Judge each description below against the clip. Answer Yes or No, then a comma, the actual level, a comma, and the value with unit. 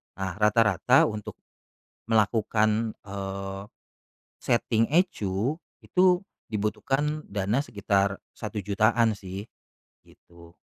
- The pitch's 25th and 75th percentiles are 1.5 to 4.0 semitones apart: Yes, average, 2.8 semitones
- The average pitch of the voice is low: Yes, low, 105 Hz